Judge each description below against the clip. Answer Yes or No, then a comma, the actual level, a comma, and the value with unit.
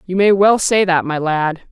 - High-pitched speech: No, medium, 180 Hz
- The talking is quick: Yes, fast, 245 wpm